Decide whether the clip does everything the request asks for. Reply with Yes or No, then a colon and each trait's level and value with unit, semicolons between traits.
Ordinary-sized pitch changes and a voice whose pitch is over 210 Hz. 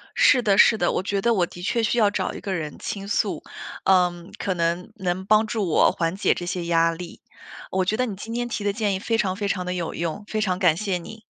No: average, 3.2 semitones; high, 190 Hz